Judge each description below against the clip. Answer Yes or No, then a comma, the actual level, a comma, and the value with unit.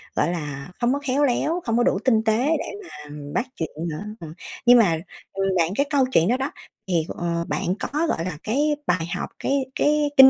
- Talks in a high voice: Yes, high, 220 Hz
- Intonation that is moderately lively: No, wide, 8.2 semitones